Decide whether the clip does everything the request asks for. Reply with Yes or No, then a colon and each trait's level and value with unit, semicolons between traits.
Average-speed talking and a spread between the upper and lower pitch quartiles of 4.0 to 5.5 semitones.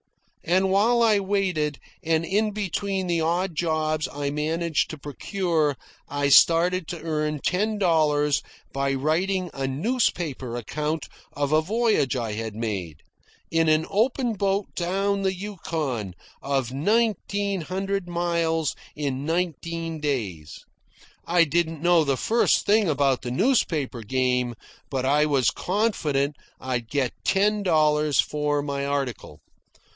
No: slow, 130 wpm; average, 5.2 semitones